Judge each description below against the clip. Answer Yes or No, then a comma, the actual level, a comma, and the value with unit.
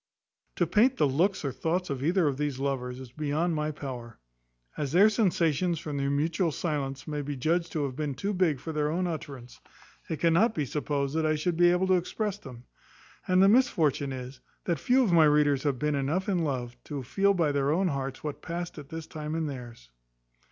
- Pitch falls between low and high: Yes, medium, 150 Hz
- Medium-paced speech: No, fast, 215 wpm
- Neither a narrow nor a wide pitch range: Yes, average, 4.0 semitones